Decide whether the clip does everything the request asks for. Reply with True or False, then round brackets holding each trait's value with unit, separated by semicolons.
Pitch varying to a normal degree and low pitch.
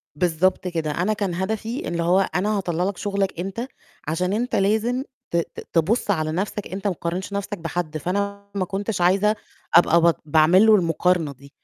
False (3.1 semitones; 185 Hz)